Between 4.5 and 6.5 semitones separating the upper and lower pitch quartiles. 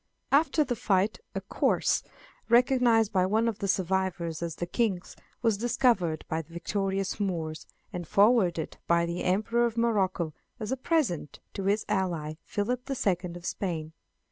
Yes: average, 5.0 semitones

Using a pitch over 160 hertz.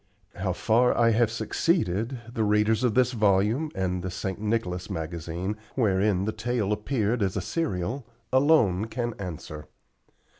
No: low, 105 Hz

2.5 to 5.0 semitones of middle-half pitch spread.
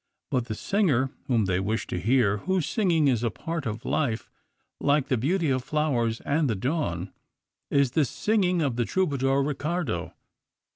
No: wide, 5.5 semitones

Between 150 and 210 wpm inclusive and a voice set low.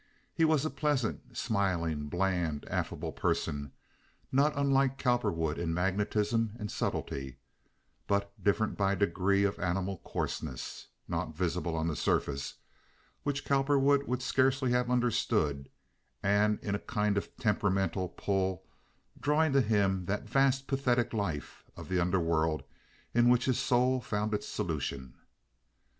No: slow, 135 wpm; low, 105 Hz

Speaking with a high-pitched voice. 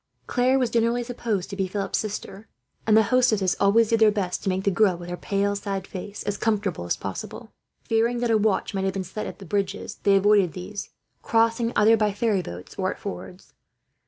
Yes: high, 205 Hz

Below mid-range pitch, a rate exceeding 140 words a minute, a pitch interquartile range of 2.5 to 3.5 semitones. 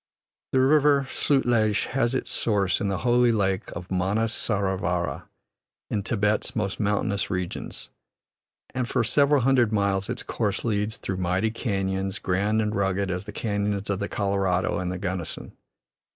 Yes: low, 100 Hz; average, 155 wpm; average, 3.2 semitones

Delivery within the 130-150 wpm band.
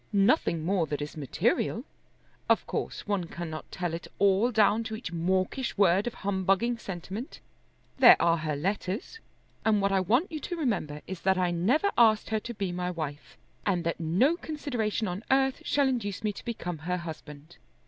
No: average, 180 wpm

